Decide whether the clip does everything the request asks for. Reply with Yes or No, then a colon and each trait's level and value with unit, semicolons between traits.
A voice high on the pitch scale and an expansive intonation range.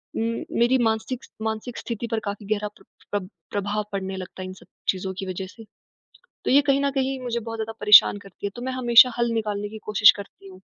No: high, 220 Hz; average, 2.9 semitones